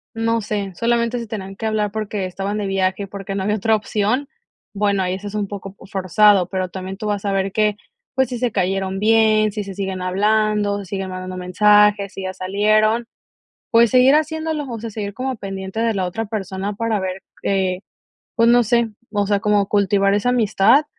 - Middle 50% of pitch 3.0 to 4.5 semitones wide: No, narrow, 2.5 semitones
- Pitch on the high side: Yes, high, 205 Hz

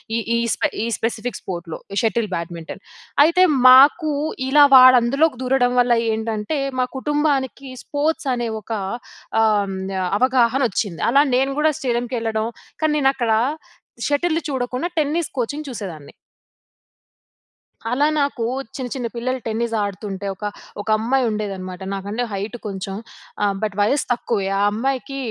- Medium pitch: No, high, 245 Hz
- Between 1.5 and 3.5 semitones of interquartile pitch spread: No, average, 4.5 semitones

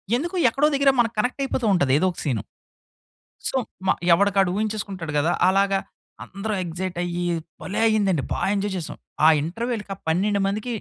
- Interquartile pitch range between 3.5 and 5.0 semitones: Yes, average, 3.8 semitones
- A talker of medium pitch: No, high, 200 Hz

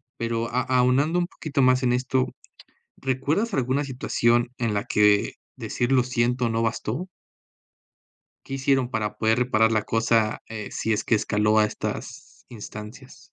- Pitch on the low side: Yes, low, 120 Hz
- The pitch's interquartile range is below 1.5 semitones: No, average, 2.8 semitones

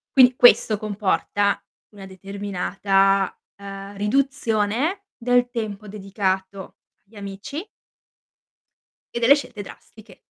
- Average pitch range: Yes, average, 3.3 semitones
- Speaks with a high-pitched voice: Yes, high, 205 Hz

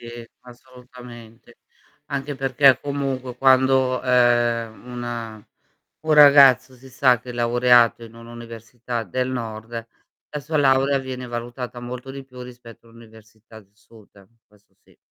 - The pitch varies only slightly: Yes, narrow, 2.2 semitones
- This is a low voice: Yes, low, 125 Hz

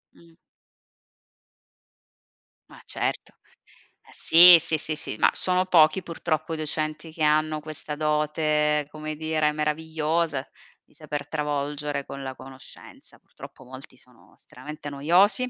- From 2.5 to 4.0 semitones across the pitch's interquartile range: No, narrow, 1.4 semitones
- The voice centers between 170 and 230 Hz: No, medium, 155 Hz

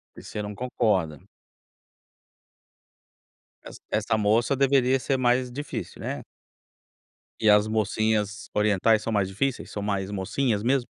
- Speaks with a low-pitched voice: Yes, low, 110 Hz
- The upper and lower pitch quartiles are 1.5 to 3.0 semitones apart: No, average, 3.4 semitones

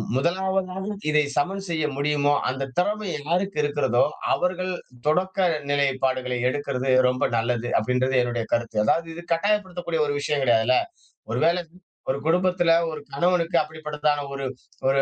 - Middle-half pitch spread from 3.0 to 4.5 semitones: No, average, 5.3 semitones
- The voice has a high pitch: No, medium, 150 Hz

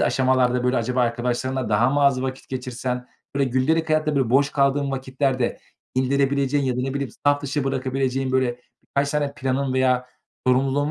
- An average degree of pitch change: No, narrow, 1.6 semitones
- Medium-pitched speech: No, low, 130 Hz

